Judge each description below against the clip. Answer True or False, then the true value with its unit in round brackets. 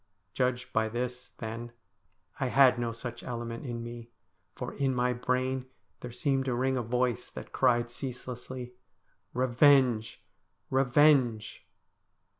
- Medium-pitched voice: False (125 Hz)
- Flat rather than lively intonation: True (1.5 semitones)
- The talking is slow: True (130 wpm)